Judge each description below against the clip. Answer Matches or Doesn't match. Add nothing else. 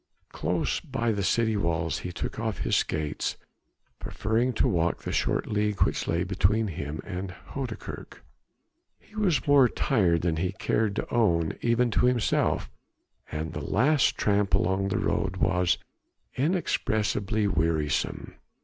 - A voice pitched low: Matches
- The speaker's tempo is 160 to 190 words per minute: Doesn't match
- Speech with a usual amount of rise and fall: Matches